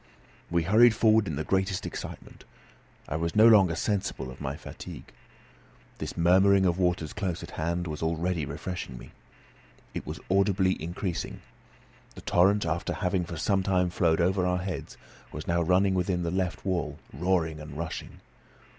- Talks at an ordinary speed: Yes, average, 165 wpm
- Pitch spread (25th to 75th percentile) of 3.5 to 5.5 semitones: No, narrow, 2.6 semitones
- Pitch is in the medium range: No, very low, 90 Hz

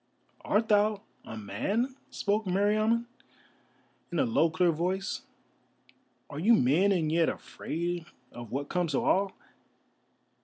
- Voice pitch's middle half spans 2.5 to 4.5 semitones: No, average, 4.9 semitones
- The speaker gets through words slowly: Yes, slow, 125 wpm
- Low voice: No, medium, 185 Hz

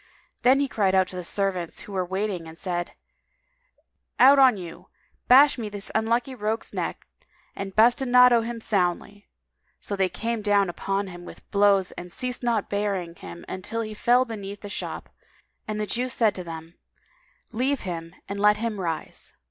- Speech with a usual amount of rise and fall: Yes, average, 4.0 semitones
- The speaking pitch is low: No, high, 205 Hz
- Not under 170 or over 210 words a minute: Yes, average, 175 wpm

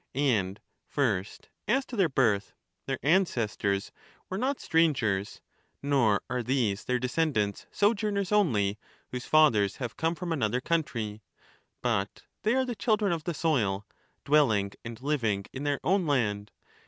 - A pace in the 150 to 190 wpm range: No, average, 140 wpm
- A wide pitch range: Yes, wide, 7.7 semitones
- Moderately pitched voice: No, low, 130 Hz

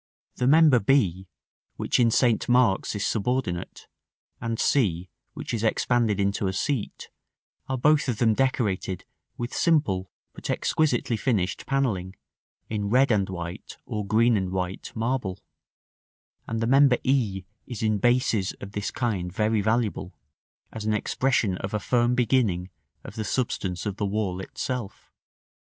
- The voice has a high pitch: No, low, 110 Hz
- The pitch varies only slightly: No, average, 4.4 semitones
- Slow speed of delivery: No, average, 145 wpm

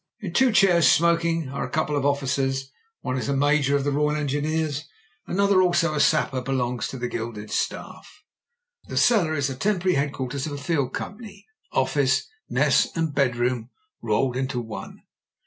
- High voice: No, medium, 145 Hz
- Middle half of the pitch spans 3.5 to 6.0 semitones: Yes, average, 3.8 semitones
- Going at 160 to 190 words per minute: Yes, average, 175 wpm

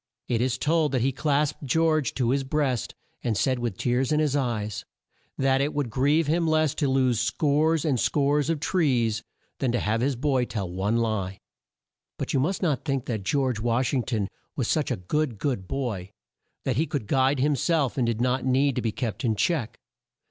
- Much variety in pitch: No, average, 3.8 semitones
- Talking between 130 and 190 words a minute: No, fast, 205 wpm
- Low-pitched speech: Yes, low, 130 Hz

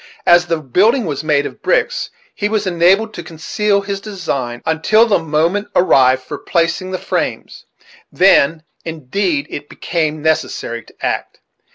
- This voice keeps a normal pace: Yes, average, 150 wpm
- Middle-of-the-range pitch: Yes, medium, 170 Hz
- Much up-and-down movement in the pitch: No, average, 4.6 semitones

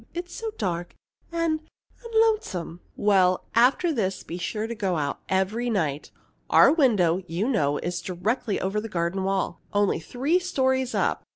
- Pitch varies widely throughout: Yes, wide, 6.6 semitones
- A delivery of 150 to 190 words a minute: Yes, average, 160 wpm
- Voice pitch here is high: Yes, high, 205 Hz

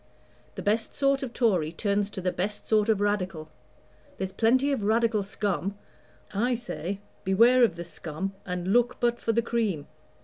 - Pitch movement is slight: No, average, 3.7 semitones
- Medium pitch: No, high, 205 Hz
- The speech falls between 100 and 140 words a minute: No, average, 170 wpm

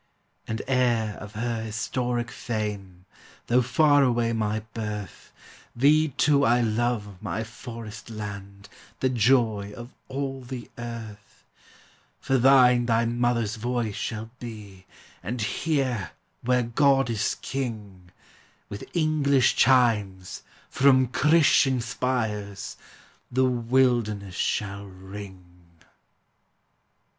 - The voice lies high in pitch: No, low, 115 Hz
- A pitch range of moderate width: Yes, average, 3.4 semitones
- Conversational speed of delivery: No, slow, 105 wpm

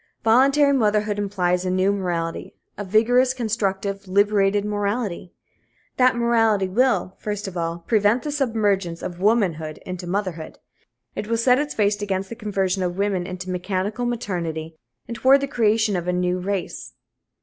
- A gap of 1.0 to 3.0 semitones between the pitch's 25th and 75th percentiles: No, average, 3.7 semitones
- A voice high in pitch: Yes, high, 205 Hz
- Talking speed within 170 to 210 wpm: No, average, 155 wpm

